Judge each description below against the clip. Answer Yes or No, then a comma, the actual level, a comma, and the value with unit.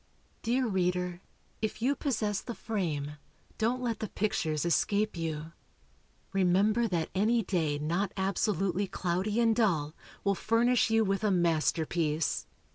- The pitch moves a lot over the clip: No, average, 4.5 semitones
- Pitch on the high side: Yes, high, 195 Hz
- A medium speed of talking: No, slow, 130 wpm